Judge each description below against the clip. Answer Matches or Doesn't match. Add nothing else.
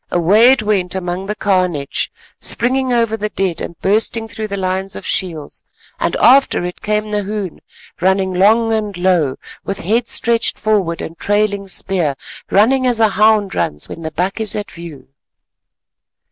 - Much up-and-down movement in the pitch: Doesn't match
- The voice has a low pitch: Doesn't match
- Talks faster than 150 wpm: Matches